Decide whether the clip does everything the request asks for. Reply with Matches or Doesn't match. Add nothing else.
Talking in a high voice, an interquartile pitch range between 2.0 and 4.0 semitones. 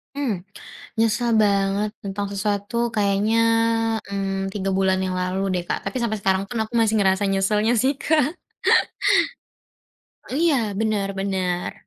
Matches